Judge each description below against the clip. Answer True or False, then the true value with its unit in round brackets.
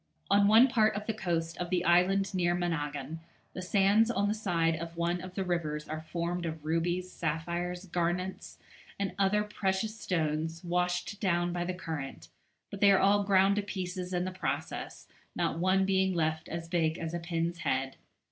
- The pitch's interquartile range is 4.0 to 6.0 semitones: False (2.6 semitones)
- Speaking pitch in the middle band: True (180 Hz)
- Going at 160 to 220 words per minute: True (185 wpm)